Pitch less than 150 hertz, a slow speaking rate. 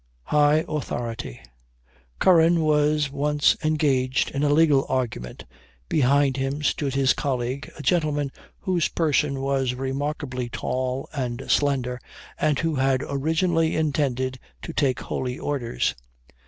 Yes: medium, 140 Hz; slow, 120 wpm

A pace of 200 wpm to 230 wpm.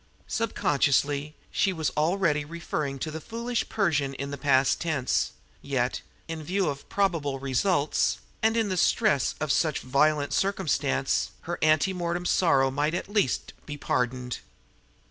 No: average, 145 wpm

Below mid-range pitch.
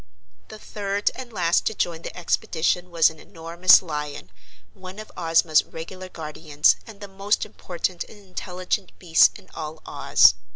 No: medium, 175 Hz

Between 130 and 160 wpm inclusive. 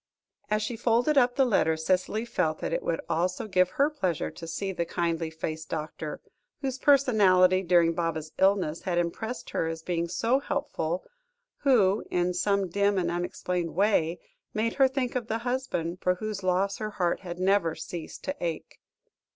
No: average, 175 wpm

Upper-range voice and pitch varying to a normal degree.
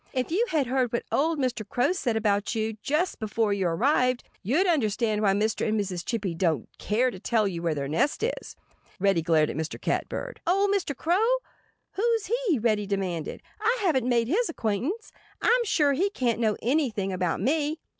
No: high, 235 Hz; wide, 7.8 semitones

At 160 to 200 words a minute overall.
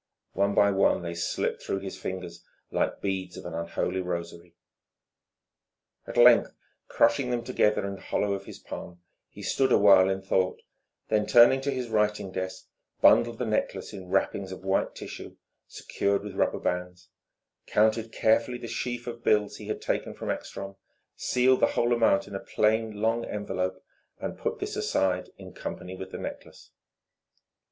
Yes: average, 170 wpm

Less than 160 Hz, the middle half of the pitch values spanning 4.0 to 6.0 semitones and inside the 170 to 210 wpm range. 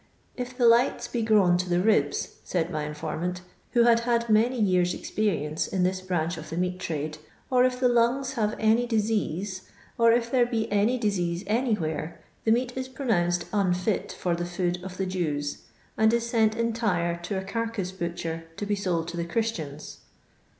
No: high, 195 Hz; average, 5.0 semitones; average, 185 wpm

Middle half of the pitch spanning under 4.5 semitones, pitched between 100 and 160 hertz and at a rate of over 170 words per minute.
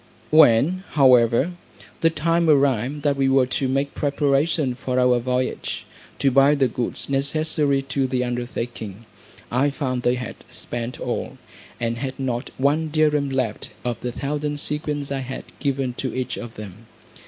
No: average, 2.8 semitones; low, 135 Hz; average, 155 wpm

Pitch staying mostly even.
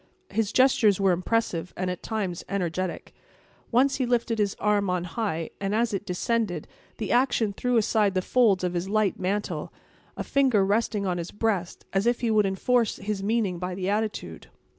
No: average, 3.6 semitones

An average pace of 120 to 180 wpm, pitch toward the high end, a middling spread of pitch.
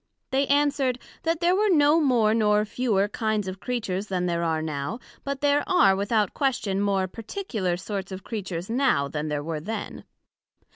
No: average, 175 wpm; high, 210 Hz; wide, 6.3 semitones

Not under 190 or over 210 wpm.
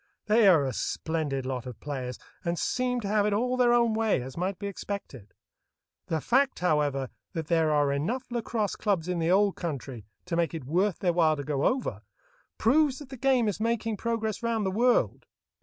Yes: average, 200 wpm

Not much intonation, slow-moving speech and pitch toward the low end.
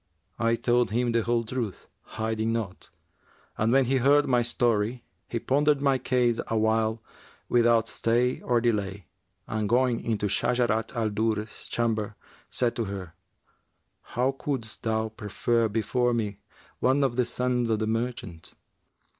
No: narrow, 1.9 semitones; average, 145 wpm; low, 115 Hz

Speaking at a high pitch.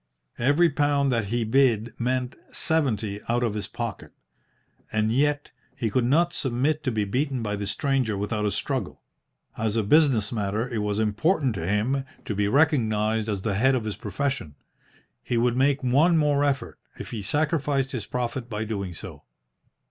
No: low, 120 Hz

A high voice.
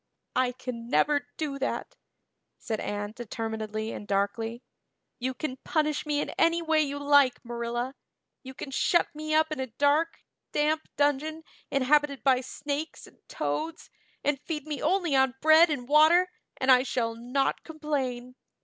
Yes: very high, 275 Hz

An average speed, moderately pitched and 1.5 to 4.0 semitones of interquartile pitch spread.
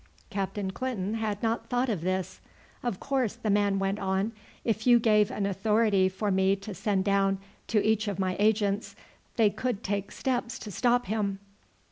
No: average, 175 wpm; high, 205 Hz; narrow, 2.5 semitones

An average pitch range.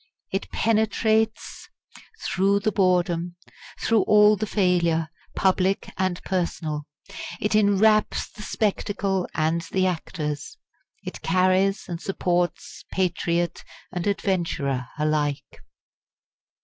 Yes: average, 3.0 semitones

